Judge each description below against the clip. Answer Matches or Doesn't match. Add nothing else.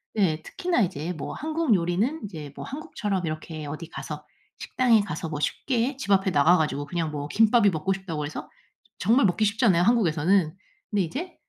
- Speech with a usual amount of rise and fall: Doesn't match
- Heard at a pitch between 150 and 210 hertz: Matches